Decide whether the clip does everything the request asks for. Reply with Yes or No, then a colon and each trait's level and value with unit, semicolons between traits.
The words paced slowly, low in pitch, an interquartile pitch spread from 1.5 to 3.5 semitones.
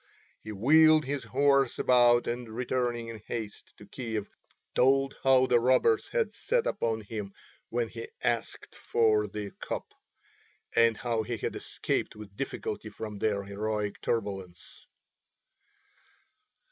Yes: slow, 130 wpm; low, 115 Hz; average, 3.2 semitones